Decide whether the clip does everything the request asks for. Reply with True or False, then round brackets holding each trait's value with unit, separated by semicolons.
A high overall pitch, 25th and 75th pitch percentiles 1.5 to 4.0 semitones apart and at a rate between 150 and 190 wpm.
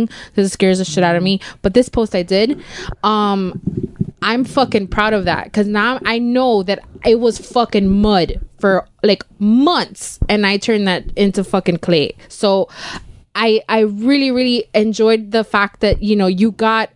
True (210 Hz; 2.5 semitones; 180 wpm)